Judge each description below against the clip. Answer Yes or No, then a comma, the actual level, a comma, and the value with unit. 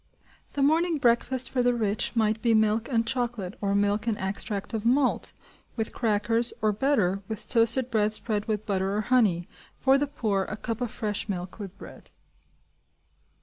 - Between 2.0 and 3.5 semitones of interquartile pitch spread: Yes, average, 2.9 semitones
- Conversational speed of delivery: Yes, average, 175 wpm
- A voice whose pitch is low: No, high, 220 Hz